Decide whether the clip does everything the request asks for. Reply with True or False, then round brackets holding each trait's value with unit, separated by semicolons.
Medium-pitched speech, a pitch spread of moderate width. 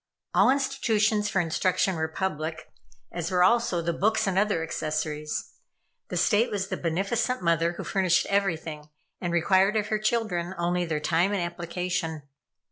True (180 Hz; 3.9 semitones)